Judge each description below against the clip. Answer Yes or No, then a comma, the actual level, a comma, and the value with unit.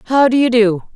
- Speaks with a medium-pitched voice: No, high, 235 Hz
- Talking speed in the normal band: No, fast, 250 wpm